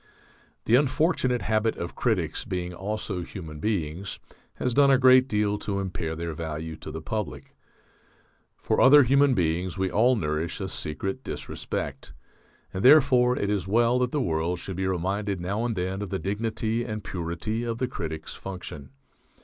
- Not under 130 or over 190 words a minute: Yes, average, 165 wpm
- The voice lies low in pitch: Yes, low, 100 Hz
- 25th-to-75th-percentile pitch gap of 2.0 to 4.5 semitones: No, wide, 5.4 semitones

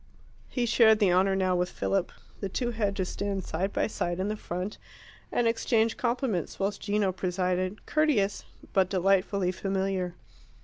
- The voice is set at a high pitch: Yes, high, 195 Hz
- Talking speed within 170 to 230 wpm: No, average, 160 wpm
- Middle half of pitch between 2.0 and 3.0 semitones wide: Yes, narrow, 2.6 semitones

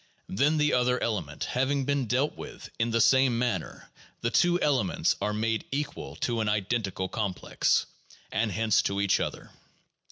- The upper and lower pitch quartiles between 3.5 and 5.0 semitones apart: Yes, average, 4.0 semitones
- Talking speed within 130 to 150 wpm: No, average, 165 wpm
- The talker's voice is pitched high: No, low, 115 Hz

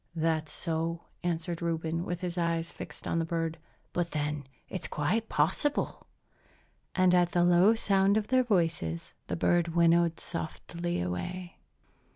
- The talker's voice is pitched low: No, medium, 170 Hz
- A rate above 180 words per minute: No, average, 145 wpm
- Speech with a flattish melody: Yes, narrow, 1.5 semitones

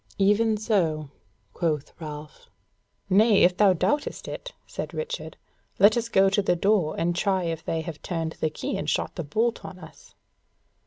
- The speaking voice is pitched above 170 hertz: Yes, medium, 185 Hz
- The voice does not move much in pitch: No, average, 4.7 semitones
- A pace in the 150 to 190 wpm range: Yes, average, 170 wpm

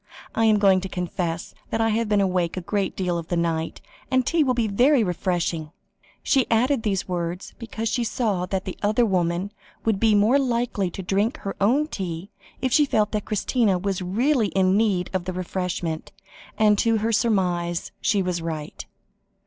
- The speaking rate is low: No, average, 180 wpm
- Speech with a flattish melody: No, average, 4.0 semitones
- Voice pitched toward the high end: Yes, high, 200 Hz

